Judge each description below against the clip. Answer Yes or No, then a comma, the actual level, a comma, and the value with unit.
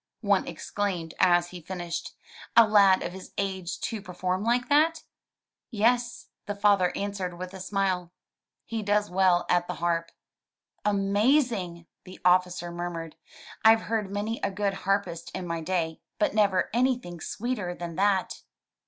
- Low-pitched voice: No, high, 190 Hz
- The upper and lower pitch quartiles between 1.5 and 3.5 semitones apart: Yes, average, 3.0 semitones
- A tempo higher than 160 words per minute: No, average, 145 wpm